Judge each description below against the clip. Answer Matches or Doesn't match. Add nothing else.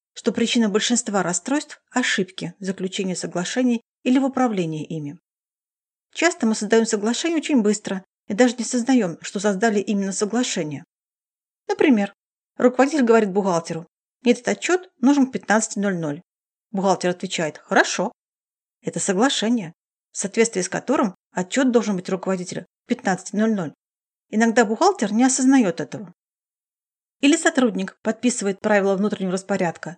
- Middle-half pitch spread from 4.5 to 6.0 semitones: Matches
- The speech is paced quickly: Doesn't match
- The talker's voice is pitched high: Matches